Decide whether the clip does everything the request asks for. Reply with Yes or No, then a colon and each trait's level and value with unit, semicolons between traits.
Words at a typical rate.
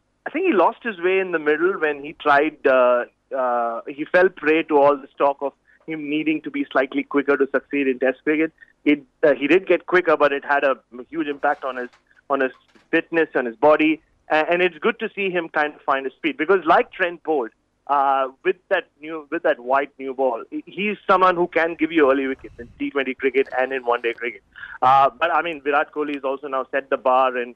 No: fast, 235 wpm